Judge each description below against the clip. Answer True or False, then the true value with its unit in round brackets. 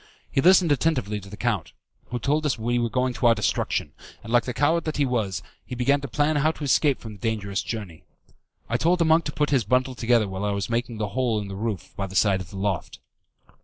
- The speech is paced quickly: True (250 wpm)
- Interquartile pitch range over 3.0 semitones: True (5.4 semitones)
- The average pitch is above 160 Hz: False (120 Hz)